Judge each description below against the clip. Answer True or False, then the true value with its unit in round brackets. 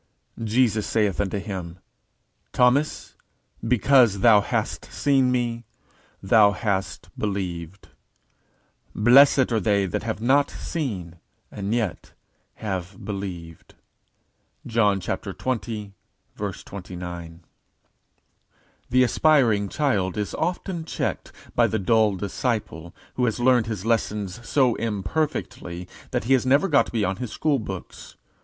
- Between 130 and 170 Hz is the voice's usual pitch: False (110 Hz)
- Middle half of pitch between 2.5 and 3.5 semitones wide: False (4.5 semitones)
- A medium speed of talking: False (110 wpm)